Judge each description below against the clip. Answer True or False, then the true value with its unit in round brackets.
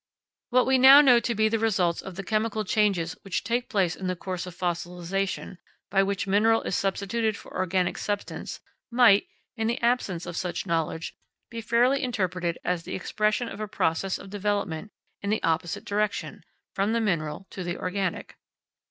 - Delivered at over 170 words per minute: True (180 wpm)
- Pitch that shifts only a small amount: False (3.7 semitones)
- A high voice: True (200 Hz)